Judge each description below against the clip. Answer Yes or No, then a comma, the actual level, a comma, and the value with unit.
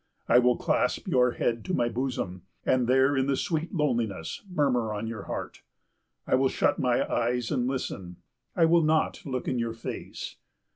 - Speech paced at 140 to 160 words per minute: No, average, 180 wpm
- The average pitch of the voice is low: Yes, low, 125 Hz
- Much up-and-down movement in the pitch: No, average, 2.8 semitones